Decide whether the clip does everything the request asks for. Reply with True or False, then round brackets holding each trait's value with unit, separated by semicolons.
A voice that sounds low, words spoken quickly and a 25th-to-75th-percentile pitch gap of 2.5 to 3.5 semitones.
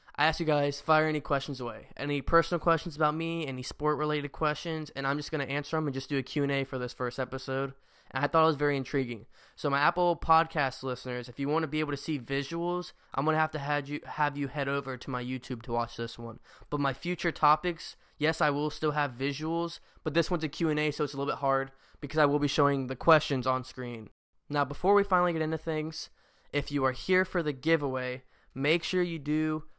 False (145 Hz; 235 wpm; 2.9 semitones)